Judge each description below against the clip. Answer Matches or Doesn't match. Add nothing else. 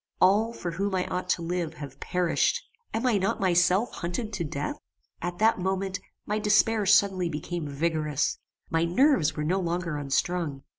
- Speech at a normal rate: Matches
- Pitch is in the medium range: Matches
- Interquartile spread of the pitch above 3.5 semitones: Doesn't match